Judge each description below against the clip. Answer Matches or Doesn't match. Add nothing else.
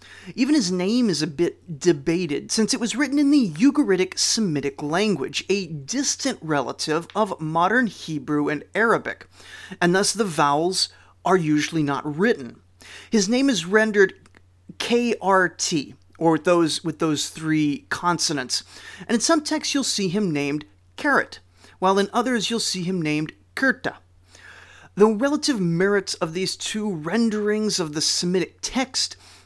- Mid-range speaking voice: Matches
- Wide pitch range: Matches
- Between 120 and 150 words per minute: Matches